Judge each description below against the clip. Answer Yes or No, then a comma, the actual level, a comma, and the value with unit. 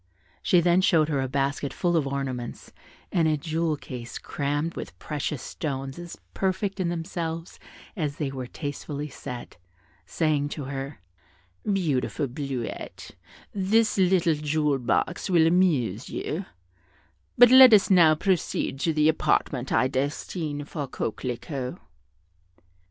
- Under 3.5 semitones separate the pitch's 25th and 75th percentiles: No, average, 4.0 semitones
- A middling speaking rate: No, slow, 130 wpm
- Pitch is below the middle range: No, medium, 150 Hz